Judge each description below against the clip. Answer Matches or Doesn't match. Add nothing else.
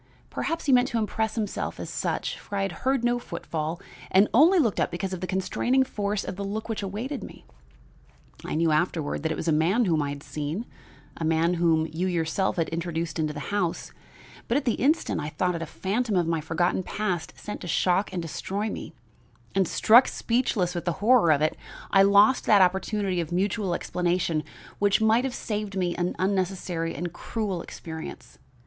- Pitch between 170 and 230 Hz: Matches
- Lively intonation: Doesn't match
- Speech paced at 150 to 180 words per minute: Doesn't match